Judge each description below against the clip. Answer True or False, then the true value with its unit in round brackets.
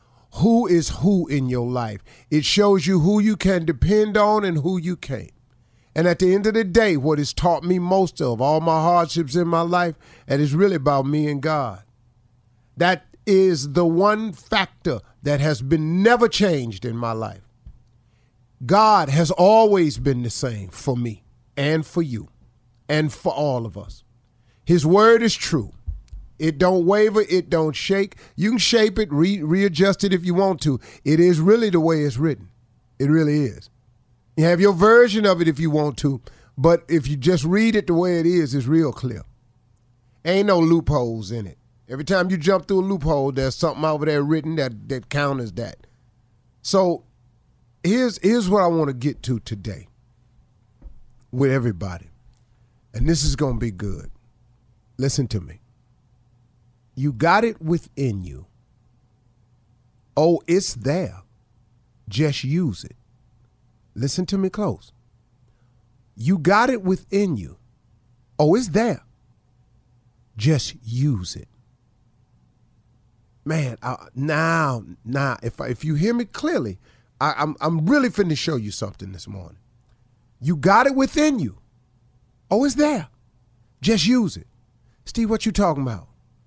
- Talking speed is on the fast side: False (160 wpm)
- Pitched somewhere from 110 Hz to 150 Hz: True (140 Hz)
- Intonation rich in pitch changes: True (6.5 semitones)